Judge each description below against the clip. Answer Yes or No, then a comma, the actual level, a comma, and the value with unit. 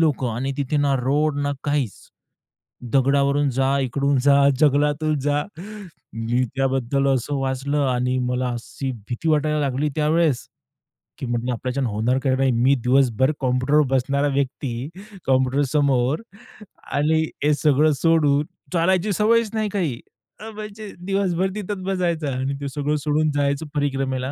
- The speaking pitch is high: No, medium, 140 Hz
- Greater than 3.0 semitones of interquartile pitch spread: No, average, 2.7 semitones